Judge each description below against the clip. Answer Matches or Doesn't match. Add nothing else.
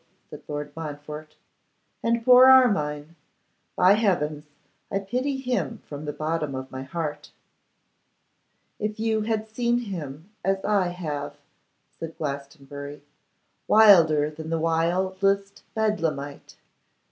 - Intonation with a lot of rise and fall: Matches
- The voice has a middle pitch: Matches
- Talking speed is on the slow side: Matches